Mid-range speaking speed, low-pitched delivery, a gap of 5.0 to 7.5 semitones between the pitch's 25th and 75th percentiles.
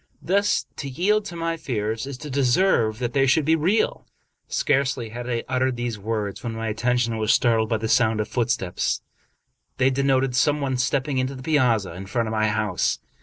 No: average, 195 wpm; low, 125 Hz; average, 3.9 semitones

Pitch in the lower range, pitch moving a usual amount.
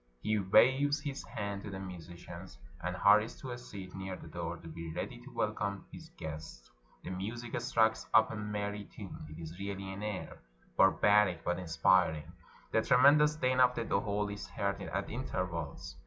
Yes: low, 100 Hz; average, 3.6 semitones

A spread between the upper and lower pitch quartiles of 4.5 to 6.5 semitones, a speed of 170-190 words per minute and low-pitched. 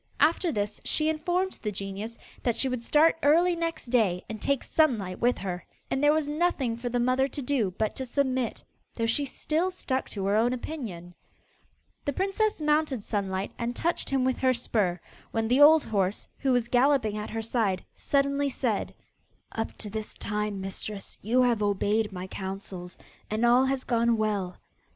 No: average, 5.2 semitones; average, 180 wpm; high, 240 Hz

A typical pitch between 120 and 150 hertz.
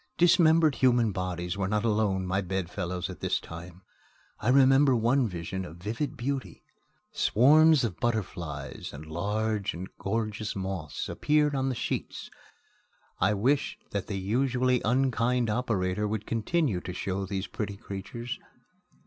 No: low, 105 Hz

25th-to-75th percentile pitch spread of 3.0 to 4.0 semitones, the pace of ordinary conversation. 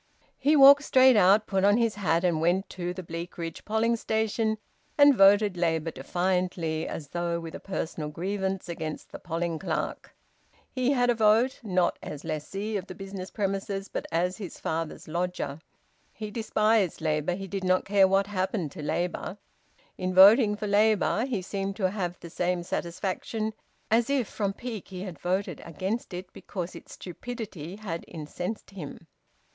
Yes: average, 3.7 semitones; average, 165 wpm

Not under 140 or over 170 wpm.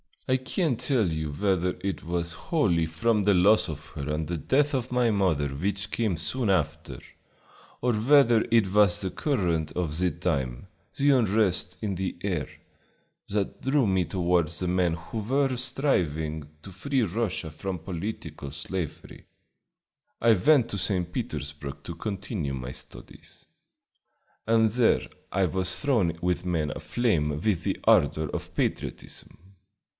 Yes: average, 150 wpm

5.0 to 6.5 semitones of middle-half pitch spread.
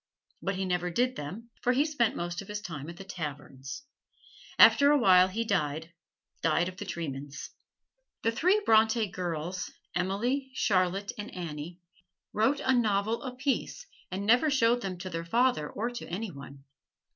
Yes: wide, 5.6 semitones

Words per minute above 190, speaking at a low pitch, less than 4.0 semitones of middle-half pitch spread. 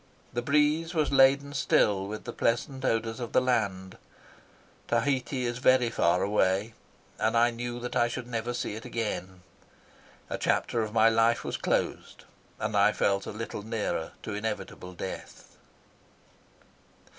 No: average, 150 wpm; low, 115 Hz; average, 3.2 semitones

